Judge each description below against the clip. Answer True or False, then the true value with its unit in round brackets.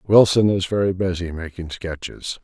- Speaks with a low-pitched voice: True (90 Hz)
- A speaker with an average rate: True (150 wpm)